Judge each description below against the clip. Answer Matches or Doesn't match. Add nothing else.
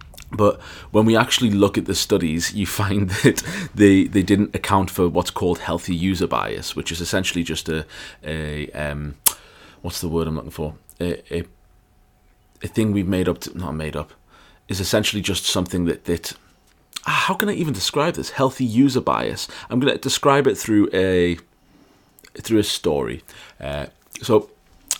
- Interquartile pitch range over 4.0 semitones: Doesn't match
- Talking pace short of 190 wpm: Matches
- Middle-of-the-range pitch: Doesn't match